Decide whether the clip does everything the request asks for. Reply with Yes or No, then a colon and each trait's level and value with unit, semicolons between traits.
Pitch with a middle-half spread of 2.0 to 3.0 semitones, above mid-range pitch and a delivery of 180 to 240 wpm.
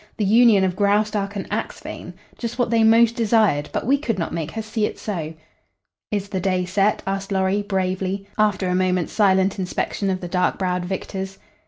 Yes: narrow, 2.4 semitones; high, 195 Hz; average, 190 wpm